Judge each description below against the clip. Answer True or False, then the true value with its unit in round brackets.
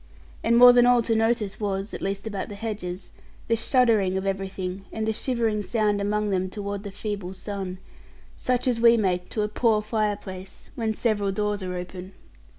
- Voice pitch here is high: True (210 Hz)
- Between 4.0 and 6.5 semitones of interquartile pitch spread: False (2.6 semitones)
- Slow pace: False (185 wpm)